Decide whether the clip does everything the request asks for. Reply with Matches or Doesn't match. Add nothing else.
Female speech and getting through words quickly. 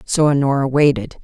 Doesn't match